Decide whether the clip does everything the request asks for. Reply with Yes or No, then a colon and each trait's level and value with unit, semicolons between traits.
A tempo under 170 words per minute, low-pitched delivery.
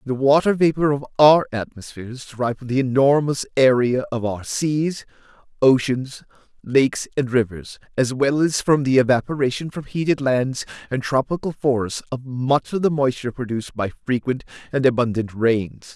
Yes: average, 160 wpm; low, 130 Hz